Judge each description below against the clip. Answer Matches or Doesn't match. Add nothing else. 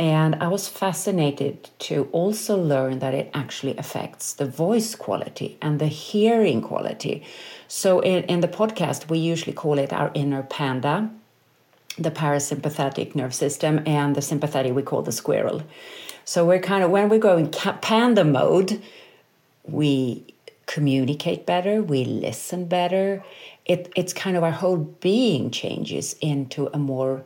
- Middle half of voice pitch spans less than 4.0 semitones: Doesn't match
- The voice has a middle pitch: Matches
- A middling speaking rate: Matches